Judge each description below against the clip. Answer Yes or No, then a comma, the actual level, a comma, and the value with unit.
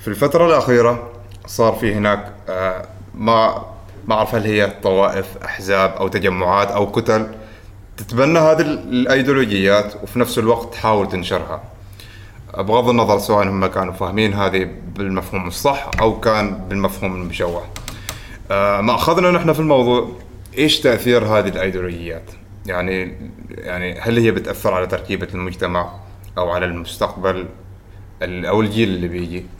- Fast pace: No, average, 125 wpm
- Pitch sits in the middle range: No, low, 100 Hz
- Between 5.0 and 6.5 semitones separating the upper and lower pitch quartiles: No, average, 3.2 semitones